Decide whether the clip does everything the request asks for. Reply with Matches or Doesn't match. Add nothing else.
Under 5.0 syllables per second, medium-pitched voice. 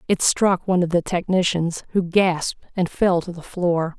Matches